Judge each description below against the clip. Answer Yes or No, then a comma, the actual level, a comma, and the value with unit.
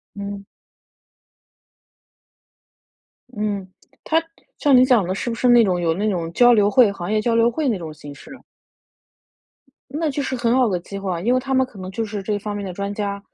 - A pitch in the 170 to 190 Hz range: No, high, 210 Hz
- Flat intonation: No, average, 4.0 semitones